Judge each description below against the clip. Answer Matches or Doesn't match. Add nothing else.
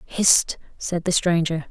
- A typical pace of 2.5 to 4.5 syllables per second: Matches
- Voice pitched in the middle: Matches